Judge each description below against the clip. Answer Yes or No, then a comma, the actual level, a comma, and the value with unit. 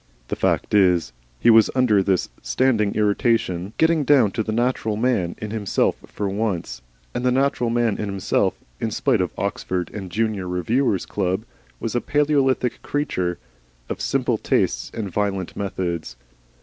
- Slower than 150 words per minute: No, average, 160 wpm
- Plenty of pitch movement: No, average, 4.5 semitones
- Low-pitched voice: Yes, low, 105 Hz